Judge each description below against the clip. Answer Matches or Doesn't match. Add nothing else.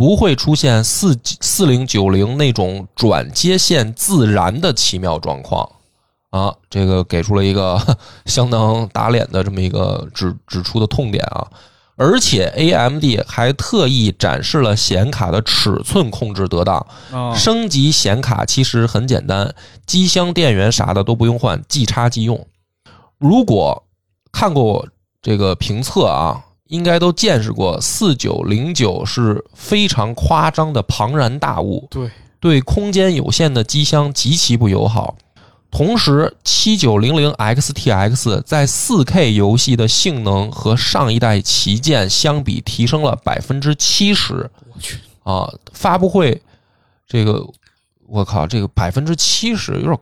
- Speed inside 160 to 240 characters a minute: Matches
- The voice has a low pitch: Matches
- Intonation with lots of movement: Matches